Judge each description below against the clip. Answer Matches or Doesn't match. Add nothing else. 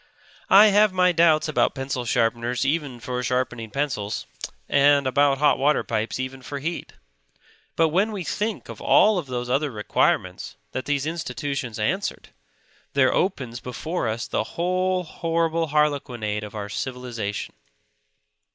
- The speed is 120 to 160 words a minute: Matches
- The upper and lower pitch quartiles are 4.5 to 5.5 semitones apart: Matches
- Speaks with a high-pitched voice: Doesn't match